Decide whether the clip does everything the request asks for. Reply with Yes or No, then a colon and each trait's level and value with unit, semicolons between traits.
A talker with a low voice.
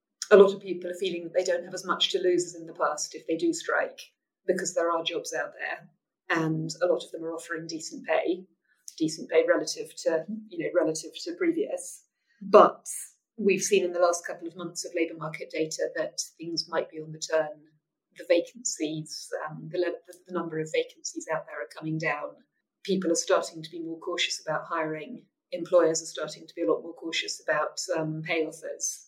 No: medium, 175 Hz